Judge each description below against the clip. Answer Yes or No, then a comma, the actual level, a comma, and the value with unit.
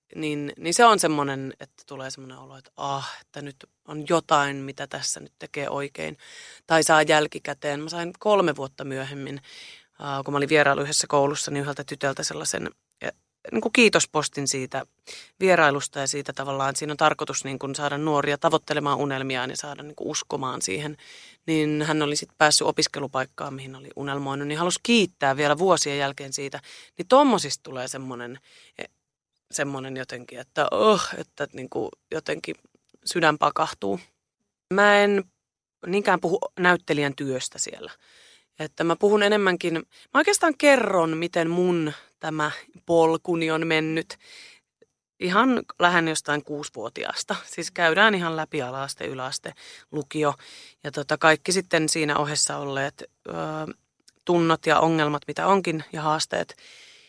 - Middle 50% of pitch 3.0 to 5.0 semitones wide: Yes, average, 3.4 semitones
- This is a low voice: No, medium, 150 Hz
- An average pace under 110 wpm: No, average, 150 wpm